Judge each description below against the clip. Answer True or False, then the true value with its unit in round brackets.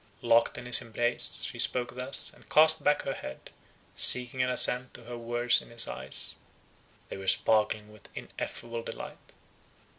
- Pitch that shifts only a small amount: True (1.6 semitones)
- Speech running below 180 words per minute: True (155 wpm)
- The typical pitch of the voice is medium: False (120 Hz)